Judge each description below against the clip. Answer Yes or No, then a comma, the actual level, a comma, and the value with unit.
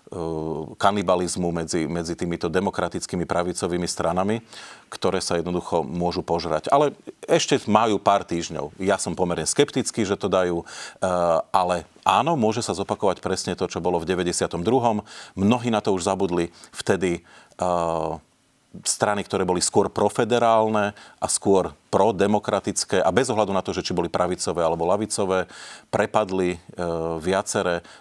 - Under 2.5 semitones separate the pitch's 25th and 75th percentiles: No, average, 2.9 semitones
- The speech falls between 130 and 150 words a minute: Yes, average, 135 wpm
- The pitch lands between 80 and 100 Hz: Yes, very low, 90 Hz